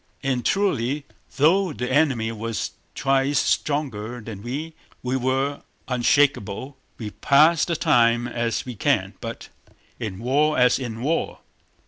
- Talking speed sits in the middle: No, slow, 130 wpm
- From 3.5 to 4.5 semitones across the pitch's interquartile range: Yes, average, 3.8 semitones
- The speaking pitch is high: No, low, 130 Hz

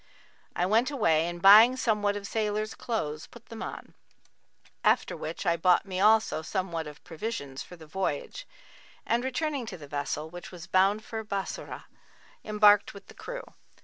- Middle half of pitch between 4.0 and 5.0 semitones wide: Yes, average, 4.7 semitones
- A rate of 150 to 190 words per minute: Yes, average, 165 wpm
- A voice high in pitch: Yes, high, 200 Hz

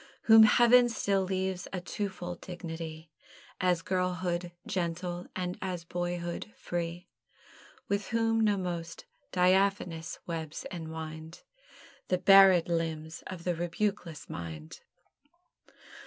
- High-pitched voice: No, medium, 175 Hz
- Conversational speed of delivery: No, slow, 105 wpm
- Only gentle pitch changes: Yes, narrow, 2.3 semitones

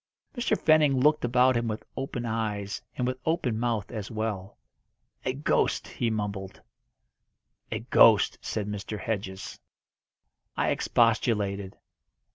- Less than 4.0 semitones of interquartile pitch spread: Yes, average, 3.6 semitones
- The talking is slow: Yes, slow, 120 wpm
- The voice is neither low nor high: No, low, 115 Hz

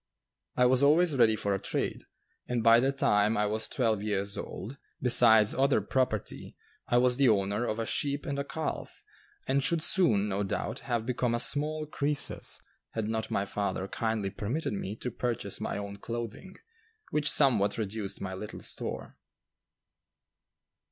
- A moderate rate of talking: Yes, average, 165 wpm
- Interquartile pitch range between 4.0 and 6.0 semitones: Yes, average, 4.7 semitones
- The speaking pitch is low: Yes, low, 115 Hz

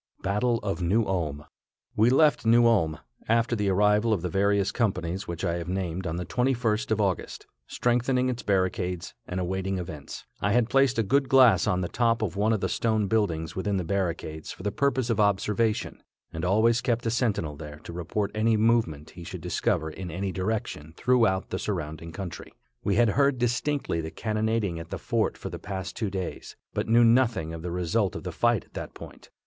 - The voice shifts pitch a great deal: No, average, 4.5 semitones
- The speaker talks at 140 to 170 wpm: No, average, 200 wpm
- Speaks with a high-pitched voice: No, low, 100 Hz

